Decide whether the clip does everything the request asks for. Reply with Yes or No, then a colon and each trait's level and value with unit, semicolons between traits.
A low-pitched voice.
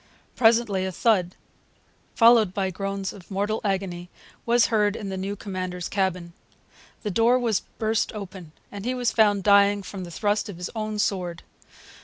No: high, 200 Hz